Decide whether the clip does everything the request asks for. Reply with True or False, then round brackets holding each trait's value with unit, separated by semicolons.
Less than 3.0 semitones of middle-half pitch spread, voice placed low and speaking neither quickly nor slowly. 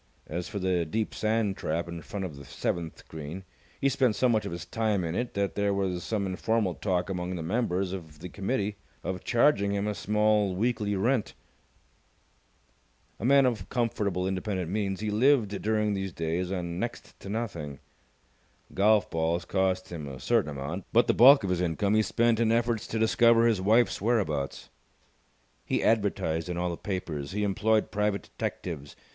False (3.8 semitones; 100 Hz; 180 wpm)